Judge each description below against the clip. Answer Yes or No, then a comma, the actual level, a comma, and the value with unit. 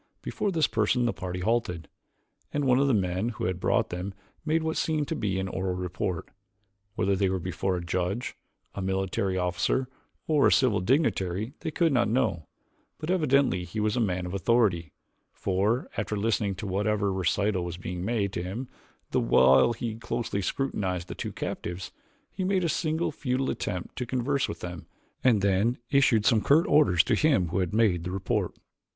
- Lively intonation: Yes, wide, 5.8 semitones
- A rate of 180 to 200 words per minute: Yes, average, 185 wpm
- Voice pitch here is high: No, low, 100 Hz